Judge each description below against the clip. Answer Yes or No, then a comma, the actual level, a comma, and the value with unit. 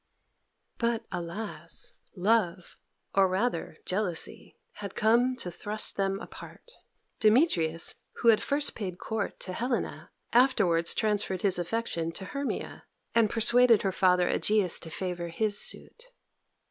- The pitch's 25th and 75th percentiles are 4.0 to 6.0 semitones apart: Yes, average, 4.3 semitones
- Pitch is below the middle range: No, high, 205 Hz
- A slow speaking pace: Yes, slow, 130 wpm